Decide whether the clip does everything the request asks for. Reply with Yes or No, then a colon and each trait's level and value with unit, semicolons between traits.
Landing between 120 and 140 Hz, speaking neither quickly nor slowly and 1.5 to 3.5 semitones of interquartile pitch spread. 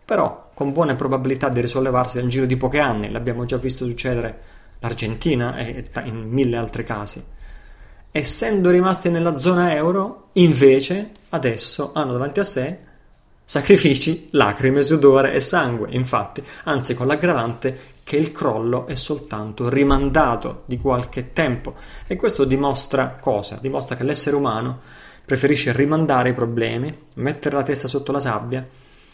Yes: low, 135 Hz; average, 140 wpm; average, 3.1 semitones